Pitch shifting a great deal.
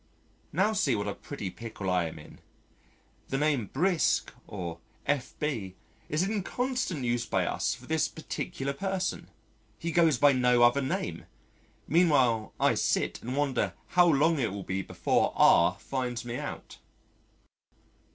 Yes: wide, 6.1 semitones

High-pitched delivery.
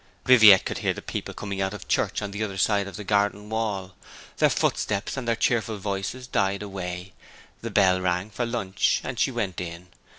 No: low, 100 Hz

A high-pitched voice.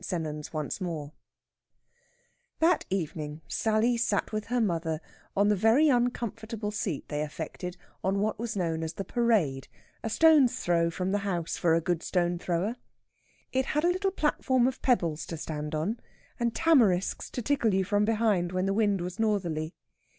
Yes: high, 195 Hz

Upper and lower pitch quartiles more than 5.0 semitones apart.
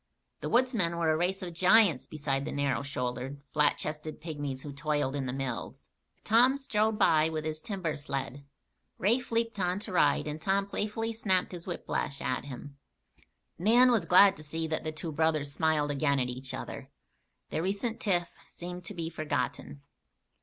Yes: wide, 5.4 semitones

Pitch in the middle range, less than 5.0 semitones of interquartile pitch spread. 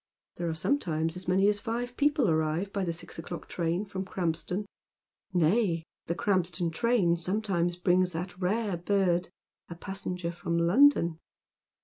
Yes: medium, 180 Hz; average, 3.0 semitones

